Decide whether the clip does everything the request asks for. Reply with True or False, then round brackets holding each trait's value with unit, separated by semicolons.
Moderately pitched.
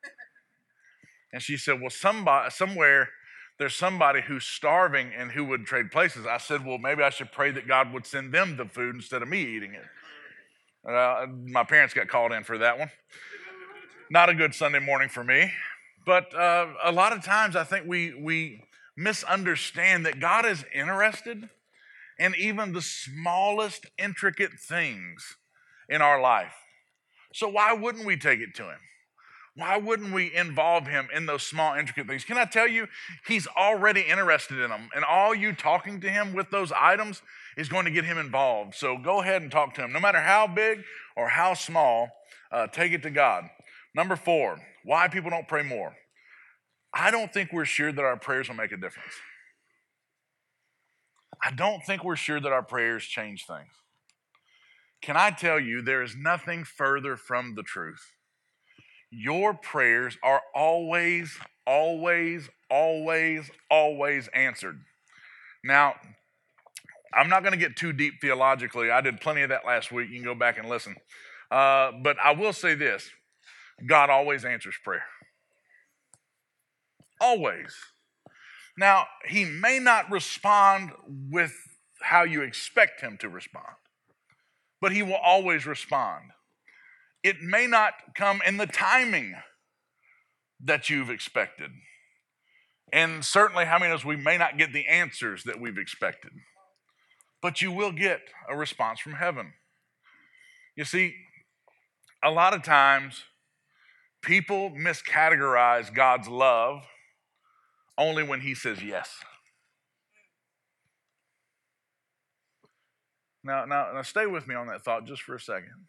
True (165 Hz)